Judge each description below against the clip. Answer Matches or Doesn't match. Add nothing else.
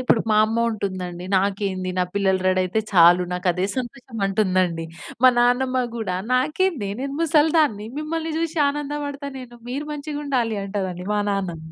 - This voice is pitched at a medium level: Doesn't match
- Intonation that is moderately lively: Doesn't match